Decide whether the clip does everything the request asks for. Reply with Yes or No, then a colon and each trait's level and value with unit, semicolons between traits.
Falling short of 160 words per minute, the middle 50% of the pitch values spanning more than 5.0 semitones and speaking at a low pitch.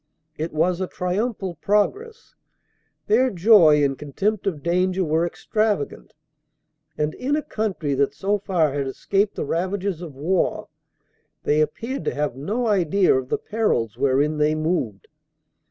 No: average, 150 wpm; wide, 5.6 semitones; medium, 180 Hz